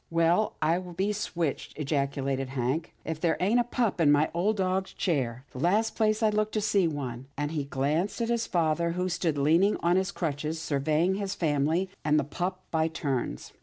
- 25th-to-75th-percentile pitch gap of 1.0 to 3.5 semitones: No, average, 4.7 semitones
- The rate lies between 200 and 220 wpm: Yes, fast, 205 wpm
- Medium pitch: Yes, medium, 165 Hz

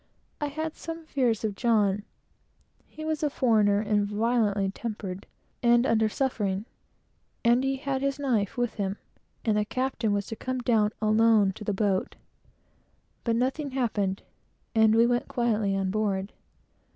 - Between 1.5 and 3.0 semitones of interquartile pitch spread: No, average, 3.7 semitones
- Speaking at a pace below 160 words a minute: Yes, average, 150 wpm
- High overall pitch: Yes, high, 225 Hz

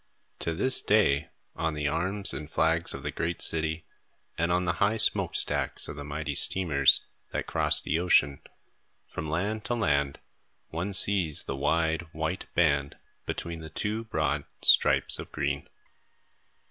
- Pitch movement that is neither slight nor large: Yes, average, 3.7 semitones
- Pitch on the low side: Yes, very low, 80 Hz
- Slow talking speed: No, average, 155 wpm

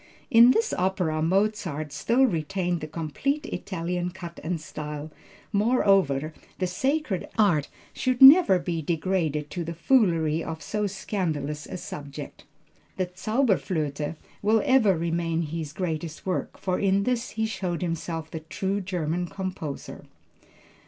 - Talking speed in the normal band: No, slow, 130 wpm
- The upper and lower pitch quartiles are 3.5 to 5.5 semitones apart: Yes, average, 4.1 semitones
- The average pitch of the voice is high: No, medium, 175 Hz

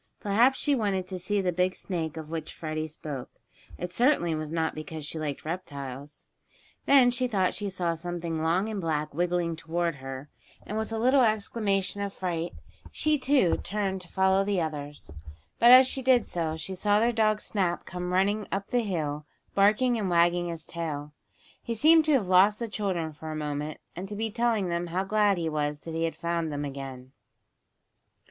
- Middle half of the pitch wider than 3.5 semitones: Yes, average, 4.7 semitones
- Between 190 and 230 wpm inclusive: Yes, average, 195 wpm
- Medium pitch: Yes, medium, 180 Hz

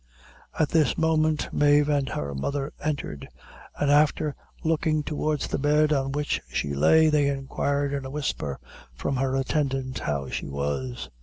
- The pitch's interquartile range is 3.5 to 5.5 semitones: No, narrow, 2.6 semitones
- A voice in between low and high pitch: Yes, medium, 145 Hz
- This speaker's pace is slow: No, average, 155 wpm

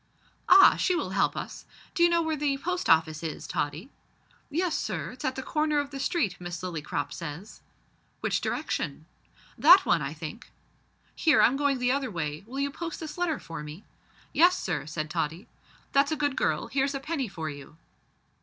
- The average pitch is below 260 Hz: No, very high, 265 Hz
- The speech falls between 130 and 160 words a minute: No, average, 185 wpm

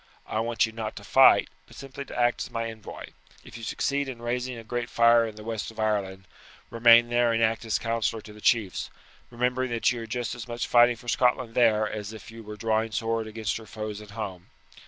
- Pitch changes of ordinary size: No, narrow, 1.6 semitones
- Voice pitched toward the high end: No, low, 115 Hz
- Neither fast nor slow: No, fast, 230 wpm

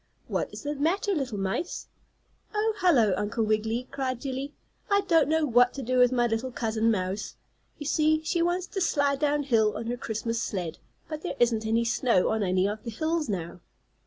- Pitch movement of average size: No, wide, 5.7 semitones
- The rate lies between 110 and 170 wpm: No, average, 195 wpm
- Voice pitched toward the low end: No, very high, 250 Hz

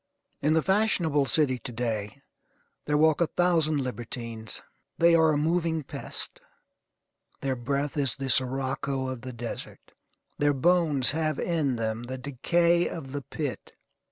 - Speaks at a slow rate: No, average, 145 wpm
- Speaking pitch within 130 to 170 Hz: Yes, medium, 140 Hz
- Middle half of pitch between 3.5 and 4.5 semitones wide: Yes, average, 4.0 semitones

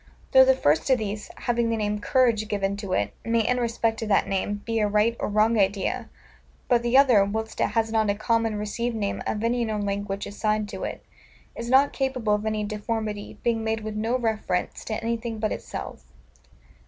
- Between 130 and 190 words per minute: No, fast, 205 wpm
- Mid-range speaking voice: No, high, 220 Hz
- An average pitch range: No, narrow, 2.0 semitones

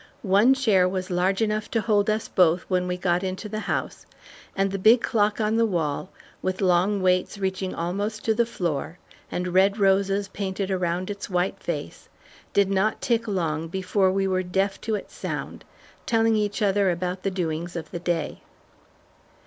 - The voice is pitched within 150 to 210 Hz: Yes, high, 190 Hz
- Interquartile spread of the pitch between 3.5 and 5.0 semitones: No, narrow, 2.4 semitones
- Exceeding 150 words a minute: Yes, average, 180 wpm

